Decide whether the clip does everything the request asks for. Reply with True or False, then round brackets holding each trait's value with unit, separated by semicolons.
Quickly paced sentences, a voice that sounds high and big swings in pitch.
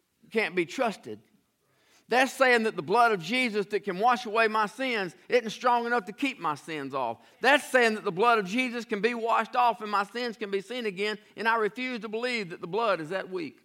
False (235 wpm; 225 Hz; 3.0 semitones)